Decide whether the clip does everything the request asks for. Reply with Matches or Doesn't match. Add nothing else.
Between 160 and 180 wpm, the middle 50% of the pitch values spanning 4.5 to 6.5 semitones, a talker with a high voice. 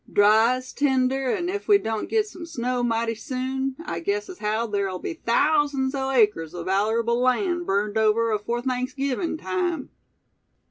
Matches